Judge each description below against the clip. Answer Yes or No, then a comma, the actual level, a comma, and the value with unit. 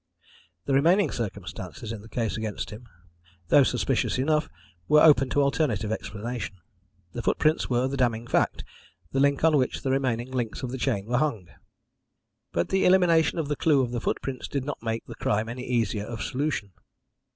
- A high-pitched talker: No, low, 125 Hz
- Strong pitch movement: No, average, 4.0 semitones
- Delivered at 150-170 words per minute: No, average, 185 wpm